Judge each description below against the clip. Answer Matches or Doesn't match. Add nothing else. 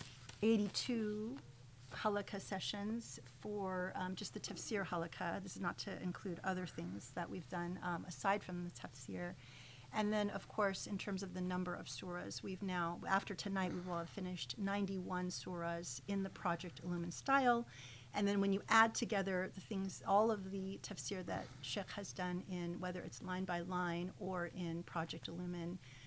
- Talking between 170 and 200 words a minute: Matches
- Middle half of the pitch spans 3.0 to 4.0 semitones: Doesn't match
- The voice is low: Doesn't match